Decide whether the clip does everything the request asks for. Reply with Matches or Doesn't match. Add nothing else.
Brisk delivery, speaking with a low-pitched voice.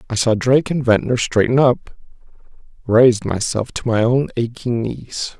Doesn't match